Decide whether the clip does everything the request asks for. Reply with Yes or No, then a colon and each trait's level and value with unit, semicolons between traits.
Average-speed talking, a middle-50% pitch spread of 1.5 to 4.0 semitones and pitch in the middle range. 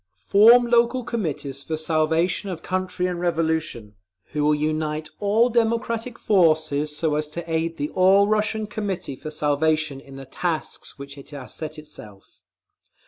No: average, 150 wpm; average, 5.0 semitones; medium, 160 Hz